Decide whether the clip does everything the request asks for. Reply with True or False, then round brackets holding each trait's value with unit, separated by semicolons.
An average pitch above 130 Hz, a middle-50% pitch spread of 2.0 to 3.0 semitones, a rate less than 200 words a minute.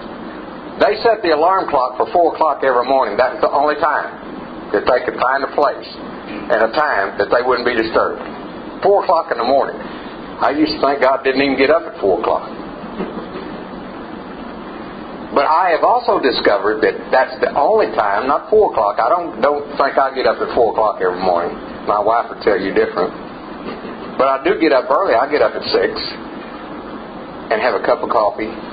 True (140 Hz; 2.4 semitones; 190 wpm)